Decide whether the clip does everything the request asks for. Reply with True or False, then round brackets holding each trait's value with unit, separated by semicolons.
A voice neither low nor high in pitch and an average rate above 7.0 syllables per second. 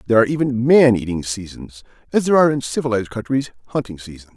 False (120 Hz; 7.4 syllables/s)